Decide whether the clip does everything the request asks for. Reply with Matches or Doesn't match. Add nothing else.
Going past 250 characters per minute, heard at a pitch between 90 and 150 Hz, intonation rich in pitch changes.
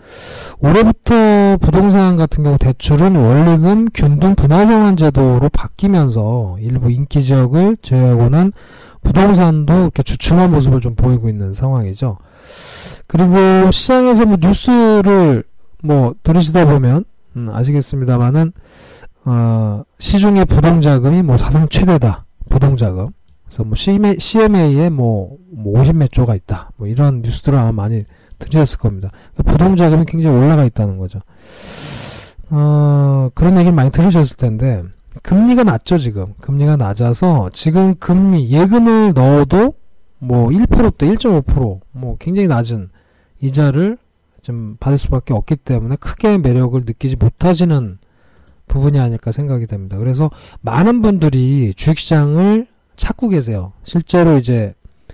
Matches